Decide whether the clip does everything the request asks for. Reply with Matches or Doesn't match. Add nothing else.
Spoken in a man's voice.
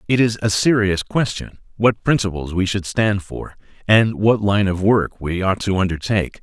Matches